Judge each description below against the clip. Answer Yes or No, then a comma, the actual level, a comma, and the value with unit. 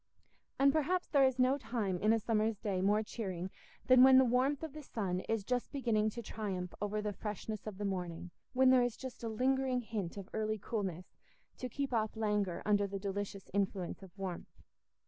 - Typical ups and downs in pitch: Yes, average, 4.3 semitones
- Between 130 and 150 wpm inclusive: No, average, 195 wpm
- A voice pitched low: No, high, 215 Hz